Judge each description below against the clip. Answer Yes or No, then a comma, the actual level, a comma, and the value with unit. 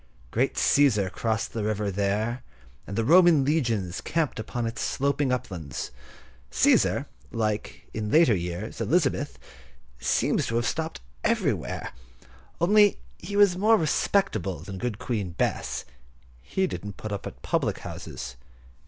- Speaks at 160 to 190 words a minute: No, slow, 135 wpm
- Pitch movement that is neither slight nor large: No, wide, 7.3 semitones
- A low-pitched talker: Yes, low, 115 Hz